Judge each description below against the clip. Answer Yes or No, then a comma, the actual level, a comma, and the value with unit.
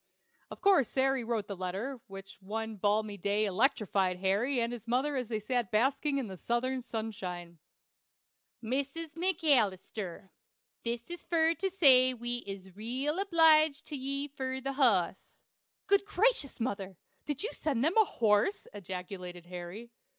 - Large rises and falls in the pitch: Yes, wide, 5.7 semitones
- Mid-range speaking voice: No, high, 240 Hz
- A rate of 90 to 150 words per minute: Yes, average, 145 wpm